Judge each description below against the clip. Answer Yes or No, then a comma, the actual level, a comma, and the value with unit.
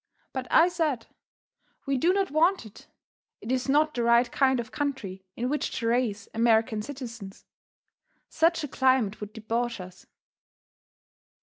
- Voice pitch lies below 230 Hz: No, high, 245 Hz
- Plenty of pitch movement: No, average, 4.3 semitones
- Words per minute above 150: No, average, 145 wpm